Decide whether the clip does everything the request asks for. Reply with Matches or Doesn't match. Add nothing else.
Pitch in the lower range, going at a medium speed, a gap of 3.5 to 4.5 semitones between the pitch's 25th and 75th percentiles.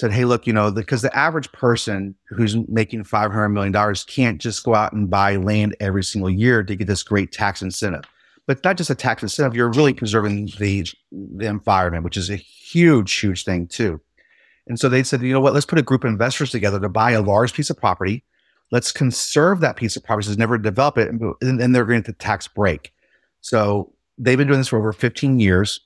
Doesn't match